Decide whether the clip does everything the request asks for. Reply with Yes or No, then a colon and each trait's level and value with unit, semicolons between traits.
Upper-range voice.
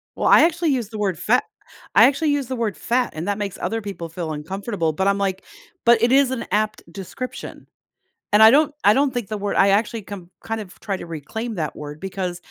Yes: high, 205 Hz